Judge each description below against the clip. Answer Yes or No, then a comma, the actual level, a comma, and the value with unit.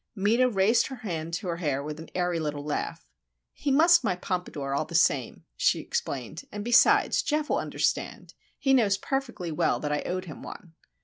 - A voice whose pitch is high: No, medium, 180 Hz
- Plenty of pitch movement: Yes, wide, 7.1 semitones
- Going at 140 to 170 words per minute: No, average, 190 wpm